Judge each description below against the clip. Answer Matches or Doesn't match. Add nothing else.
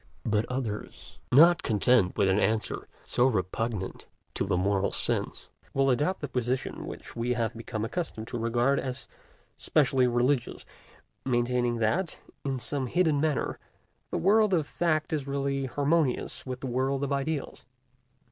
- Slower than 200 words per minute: Matches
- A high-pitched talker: Doesn't match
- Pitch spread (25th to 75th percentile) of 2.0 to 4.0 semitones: Matches